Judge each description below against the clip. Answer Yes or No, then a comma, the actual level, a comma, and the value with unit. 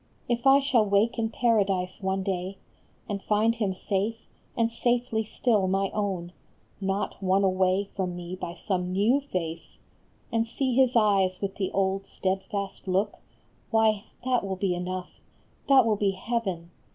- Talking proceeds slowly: No, average, 155 wpm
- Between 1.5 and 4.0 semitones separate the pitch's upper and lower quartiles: Yes, average, 3.3 semitones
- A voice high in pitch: Yes, high, 200 Hz